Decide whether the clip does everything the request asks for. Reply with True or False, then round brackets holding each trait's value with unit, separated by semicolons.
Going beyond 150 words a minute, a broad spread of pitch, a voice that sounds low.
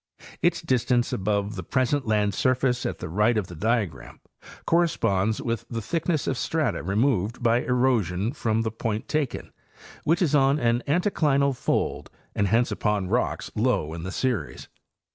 False (160 wpm; 4.3 semitones; 115 Hz)